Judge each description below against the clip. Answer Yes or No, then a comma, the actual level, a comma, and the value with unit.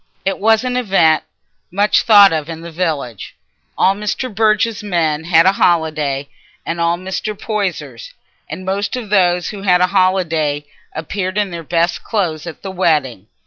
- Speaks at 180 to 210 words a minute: No, average, 165 wpm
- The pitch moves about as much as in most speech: Yes, average, 3.9 semitones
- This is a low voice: No, medium, 180 Hz